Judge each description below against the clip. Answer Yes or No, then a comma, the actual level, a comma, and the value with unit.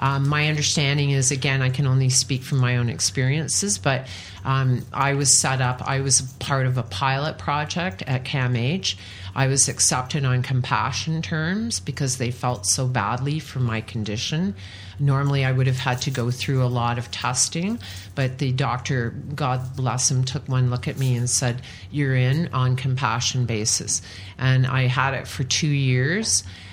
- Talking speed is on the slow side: No, average, 175 wpm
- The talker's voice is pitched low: Yes, low, 130 Hz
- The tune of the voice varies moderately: No, narrow, 2.3 semitones